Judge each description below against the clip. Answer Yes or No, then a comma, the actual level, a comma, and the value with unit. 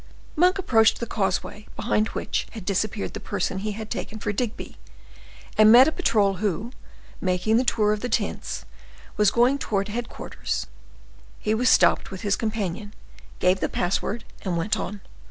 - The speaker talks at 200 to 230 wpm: No, average, 165 wpm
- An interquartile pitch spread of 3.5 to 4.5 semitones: No, average, 2.7 semitones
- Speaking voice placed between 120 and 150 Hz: No, high, 215 Hz